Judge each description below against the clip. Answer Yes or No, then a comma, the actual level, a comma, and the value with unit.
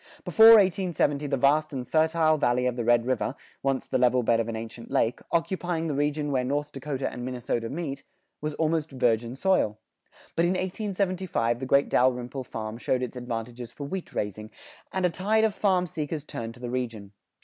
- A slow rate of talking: No, average, 190 wpm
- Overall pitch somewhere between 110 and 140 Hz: Yes, low, 135 Hz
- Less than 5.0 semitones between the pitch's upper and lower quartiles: No, average, 5.3 semitones